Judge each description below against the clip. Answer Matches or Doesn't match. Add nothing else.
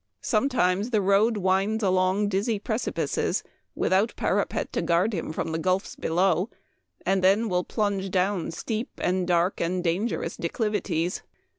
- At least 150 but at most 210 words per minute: Doesn't match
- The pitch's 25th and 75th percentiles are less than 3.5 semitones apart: Matches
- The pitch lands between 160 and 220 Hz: Matches